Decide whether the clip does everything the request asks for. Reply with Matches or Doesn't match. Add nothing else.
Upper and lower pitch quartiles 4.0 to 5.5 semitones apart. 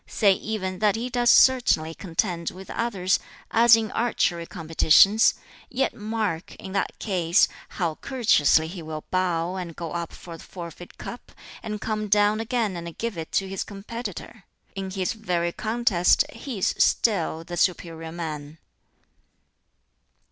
Matches